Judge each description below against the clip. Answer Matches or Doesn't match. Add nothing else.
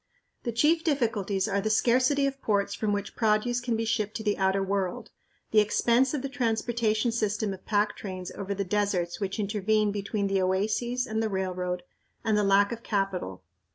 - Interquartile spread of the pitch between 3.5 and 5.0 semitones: Doesn't match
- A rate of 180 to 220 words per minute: Matches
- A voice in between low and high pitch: Doesn't match